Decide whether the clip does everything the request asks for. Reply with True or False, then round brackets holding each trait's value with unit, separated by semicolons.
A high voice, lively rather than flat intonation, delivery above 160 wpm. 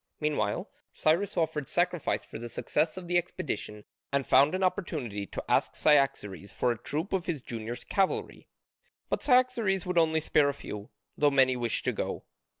False (150 Hz; 6.5 semitones; 170 wpm)